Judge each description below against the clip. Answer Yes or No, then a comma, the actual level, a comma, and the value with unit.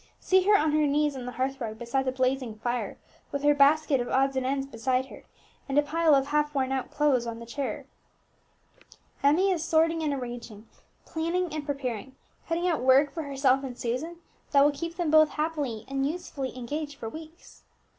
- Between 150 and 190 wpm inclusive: No, average, 200 wpm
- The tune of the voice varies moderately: Yes, average, 3.2 semitones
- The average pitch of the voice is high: Yes, very high, 280 Hz